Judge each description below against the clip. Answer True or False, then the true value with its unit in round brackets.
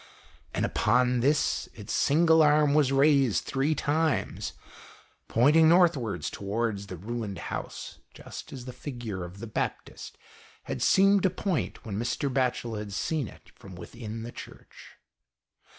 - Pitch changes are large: True (6.0 semitones)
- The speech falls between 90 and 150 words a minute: True (140 wpm)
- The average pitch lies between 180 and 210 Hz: False (125 Hz)